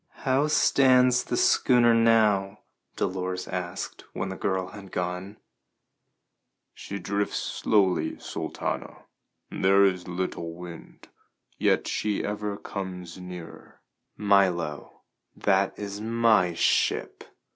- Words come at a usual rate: No, slow, 105 wpm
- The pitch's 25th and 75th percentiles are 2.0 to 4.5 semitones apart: Yes, average, 2.7 semitones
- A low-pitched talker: Yes, very low, 95 Hz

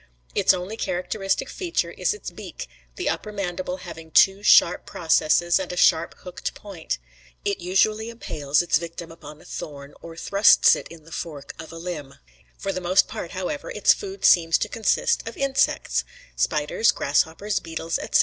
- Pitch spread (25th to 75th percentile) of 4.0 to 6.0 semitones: No, average, 3.6 semitones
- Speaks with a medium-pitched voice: Yes, medium, 180 Hz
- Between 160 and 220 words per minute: Yes, average, 170 wpm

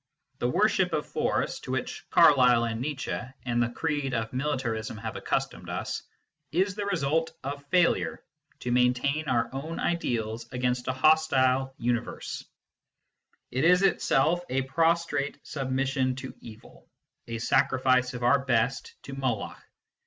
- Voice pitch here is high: No, low, 130 Hz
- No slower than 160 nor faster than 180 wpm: No, average, 140 wpm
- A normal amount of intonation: Yes, average, 3.5 semitones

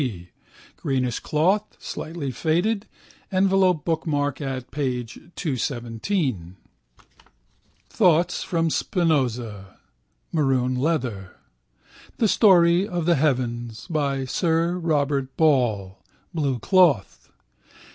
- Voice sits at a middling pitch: Yes, medium, 145 Hz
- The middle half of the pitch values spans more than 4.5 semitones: Yes, wide, 5.4 semitones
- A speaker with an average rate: No, slow, 85 wpm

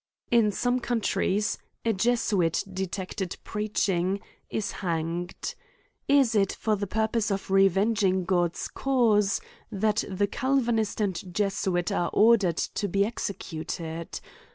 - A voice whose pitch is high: Yes, high, 200 Hz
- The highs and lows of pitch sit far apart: No, average, 3.2 semitones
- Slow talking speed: Yes, slow, 120 wpm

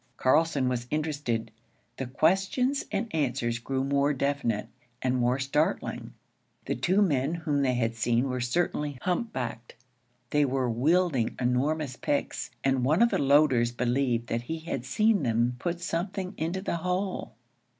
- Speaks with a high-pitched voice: No, medium, 140 Hz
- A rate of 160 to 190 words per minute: No, average, 150 wpm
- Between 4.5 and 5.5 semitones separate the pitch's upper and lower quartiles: Yes, average, 5.0 semitones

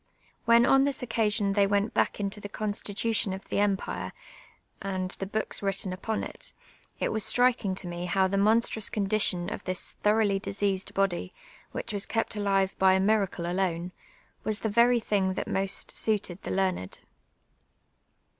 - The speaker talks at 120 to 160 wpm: No, average, 175 wpm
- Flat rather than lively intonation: Yes, narrow, 2.3 semitones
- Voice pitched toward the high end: Yes, high, 200 Hz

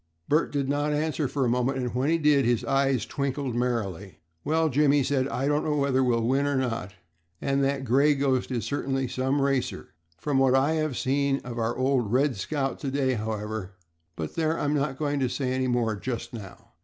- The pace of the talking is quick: Yes, fast, 210 wpm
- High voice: No, low, 135 Hz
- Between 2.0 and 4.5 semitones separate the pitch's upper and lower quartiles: Yes, average, 2.7 semitones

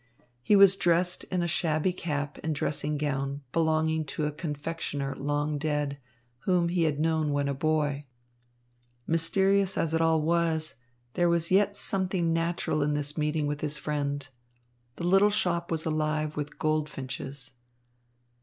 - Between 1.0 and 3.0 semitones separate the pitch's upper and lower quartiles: Yes, narrow, 2.5 semitones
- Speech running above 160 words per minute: No, average, 150 wpm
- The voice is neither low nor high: Yes, medium, 155 Hz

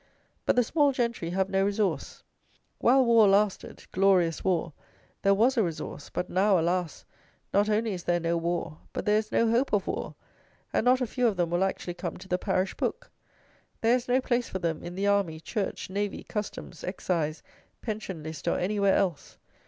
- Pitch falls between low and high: No, high, 195 Hz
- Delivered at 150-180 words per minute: No, average, 190 wpm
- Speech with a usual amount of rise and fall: Yes, average, 4.0 semitones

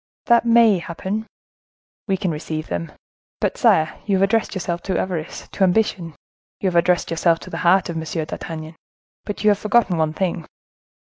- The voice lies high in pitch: No, medium, 180 Hz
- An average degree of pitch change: Yes, average, 3.5 semitones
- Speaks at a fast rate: No, average, 180 wpm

